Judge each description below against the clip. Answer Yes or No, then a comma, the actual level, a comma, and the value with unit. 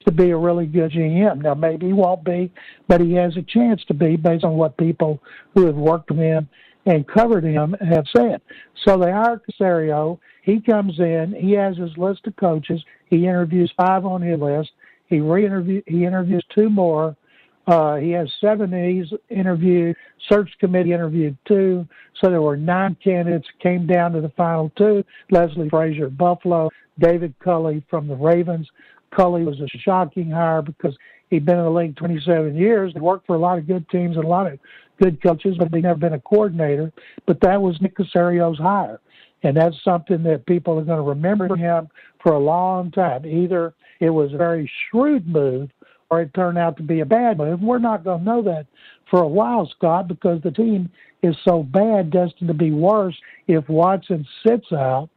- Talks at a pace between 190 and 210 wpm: Yes, average, 195 wpm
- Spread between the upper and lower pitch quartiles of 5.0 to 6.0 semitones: No, narrow, 2.5 semitones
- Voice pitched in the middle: Yes, medium, 175 Hz